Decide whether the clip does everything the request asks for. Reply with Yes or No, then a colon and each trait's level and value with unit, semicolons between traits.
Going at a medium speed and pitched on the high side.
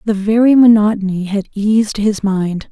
Yes: average, 155 wpm; high, 210 Hz